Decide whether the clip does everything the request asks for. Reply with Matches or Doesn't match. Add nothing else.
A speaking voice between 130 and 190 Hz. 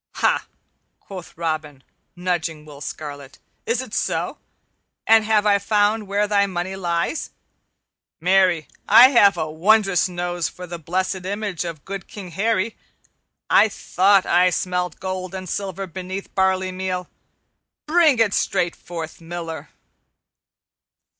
Matches